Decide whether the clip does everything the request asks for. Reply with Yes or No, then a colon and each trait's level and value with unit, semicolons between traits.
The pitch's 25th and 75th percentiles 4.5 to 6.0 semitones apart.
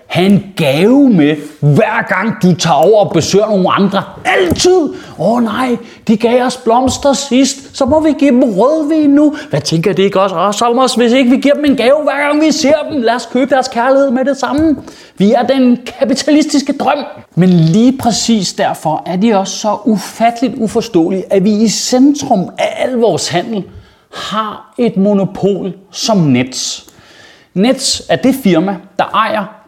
Yes: wide, 5.4 semitones